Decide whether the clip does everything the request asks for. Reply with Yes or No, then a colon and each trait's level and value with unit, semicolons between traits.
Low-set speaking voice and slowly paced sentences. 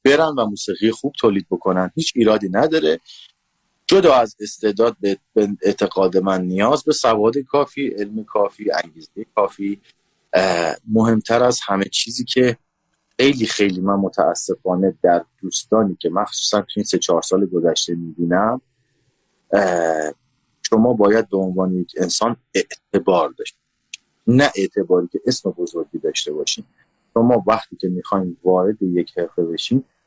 No: low, 105 Hz; average, 130 wpm